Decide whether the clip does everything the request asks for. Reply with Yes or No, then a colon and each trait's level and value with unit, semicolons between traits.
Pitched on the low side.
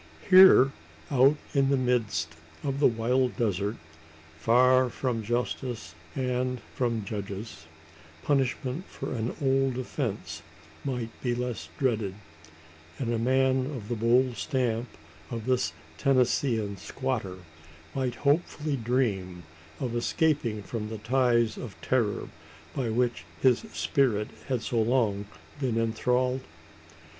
Yes: low, 125 Hz